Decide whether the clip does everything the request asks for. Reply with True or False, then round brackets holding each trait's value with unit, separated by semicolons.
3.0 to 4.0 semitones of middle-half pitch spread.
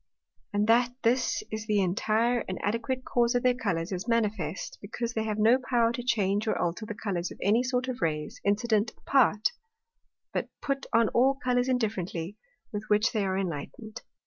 True (3.3 semitones)